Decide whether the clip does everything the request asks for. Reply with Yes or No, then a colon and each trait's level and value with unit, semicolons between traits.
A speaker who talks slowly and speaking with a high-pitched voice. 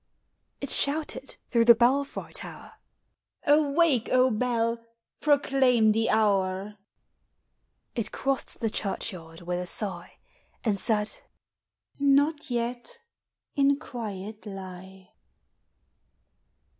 Yes: slow, 100 wpm; high, 230 Hz